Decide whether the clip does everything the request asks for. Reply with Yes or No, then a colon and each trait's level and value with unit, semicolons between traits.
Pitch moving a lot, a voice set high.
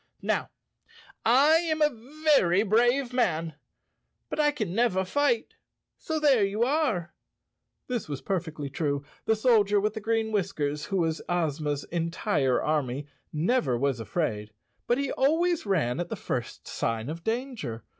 Yes: wide, 8.6 semitones; high, 195 Hz